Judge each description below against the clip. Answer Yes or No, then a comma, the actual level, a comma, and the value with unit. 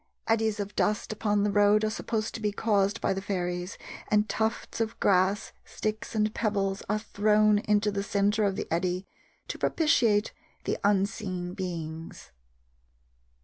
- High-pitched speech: Yes, high, 205 Hz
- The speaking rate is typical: Yes, average, 150 wpm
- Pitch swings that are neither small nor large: No, narrow, 1.7 semitones